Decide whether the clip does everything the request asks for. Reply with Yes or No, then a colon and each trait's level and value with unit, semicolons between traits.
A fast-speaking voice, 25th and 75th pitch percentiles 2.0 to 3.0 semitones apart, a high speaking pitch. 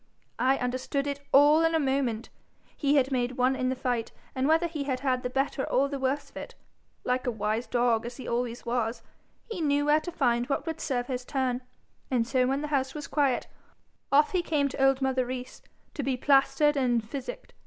Yes: fast, 215 wpm; narrow, 2.4 semitones; very high, 265 Hz